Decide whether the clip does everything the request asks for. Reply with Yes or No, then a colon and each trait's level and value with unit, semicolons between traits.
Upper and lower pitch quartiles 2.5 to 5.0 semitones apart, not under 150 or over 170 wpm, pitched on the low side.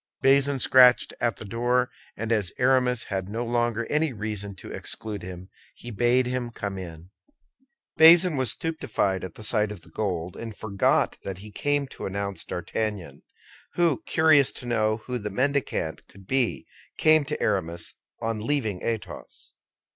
Yes: average, 4.5 semitones; average, 160 wpm; low, 115 Hz